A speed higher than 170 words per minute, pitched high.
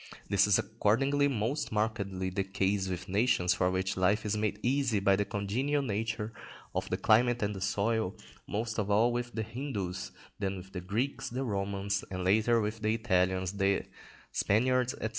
No: average, 180 wpm; low, 105 Hz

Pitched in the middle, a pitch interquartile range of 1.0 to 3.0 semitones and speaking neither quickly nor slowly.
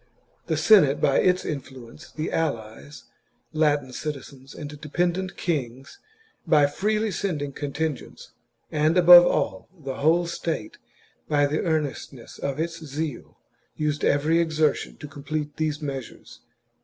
No: medium, 150 Hz; average, 2.7 semitones; slow, 125 wpm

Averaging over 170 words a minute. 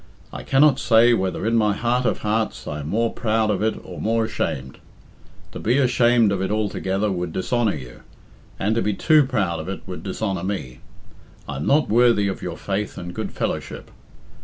Yes: average, 195 wpm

